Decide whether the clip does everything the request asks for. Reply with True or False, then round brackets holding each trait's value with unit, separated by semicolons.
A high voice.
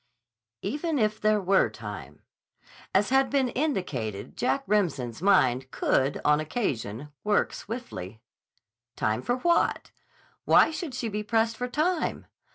True (205 Hz)